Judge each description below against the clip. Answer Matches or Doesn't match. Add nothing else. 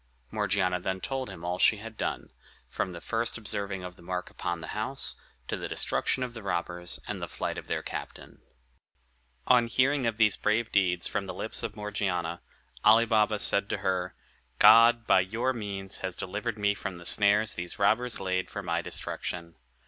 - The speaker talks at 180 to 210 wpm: Matches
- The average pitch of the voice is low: Matches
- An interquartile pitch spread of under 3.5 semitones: Doesn't match